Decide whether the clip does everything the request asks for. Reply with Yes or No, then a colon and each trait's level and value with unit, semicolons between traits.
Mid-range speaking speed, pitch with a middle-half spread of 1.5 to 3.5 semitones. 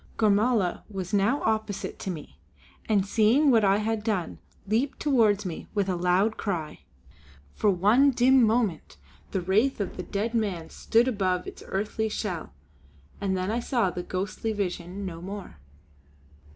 Yes: average, 155 wpm; average, 3.2 semitones